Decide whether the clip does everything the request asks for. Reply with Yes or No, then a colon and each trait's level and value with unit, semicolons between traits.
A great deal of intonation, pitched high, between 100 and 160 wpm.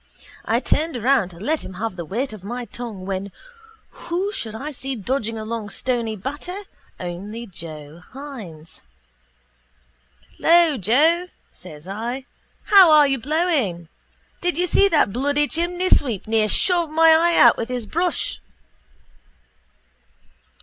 Yes: wide, 7.4 semitones; high, 245 Hz; slow, 135 wpm